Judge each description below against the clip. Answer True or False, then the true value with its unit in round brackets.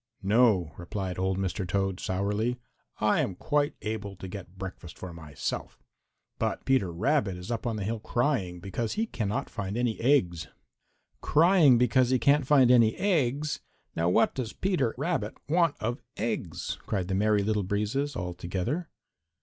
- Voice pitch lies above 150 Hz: False (110 Hz)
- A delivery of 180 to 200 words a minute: False (160 wpm)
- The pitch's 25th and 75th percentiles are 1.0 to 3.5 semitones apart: False (5.5 semitones)